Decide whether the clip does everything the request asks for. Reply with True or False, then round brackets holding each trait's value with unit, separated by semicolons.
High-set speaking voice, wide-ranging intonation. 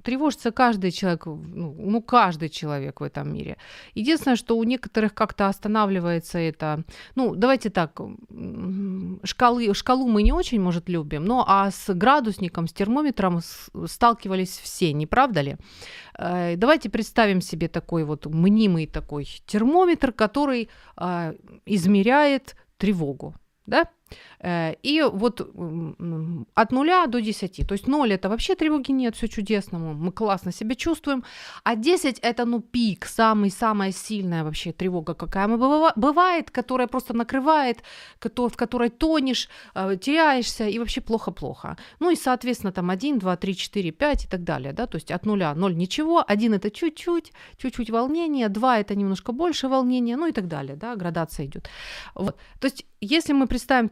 True (215 Hz; 5.8 semitones)